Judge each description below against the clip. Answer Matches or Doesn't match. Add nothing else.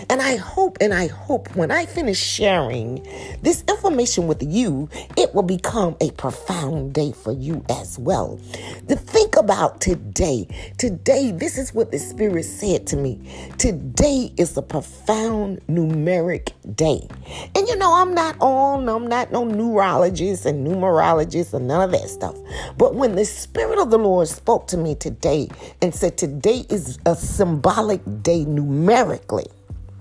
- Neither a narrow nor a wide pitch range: Doesn't match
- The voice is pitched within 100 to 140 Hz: Doesn't match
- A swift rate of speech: Doesn't match